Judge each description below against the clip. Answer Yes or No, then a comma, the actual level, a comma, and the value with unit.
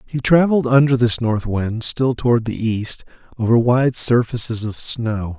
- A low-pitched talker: Yes, low, 120 Hz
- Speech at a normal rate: Yes, average, 165 wpm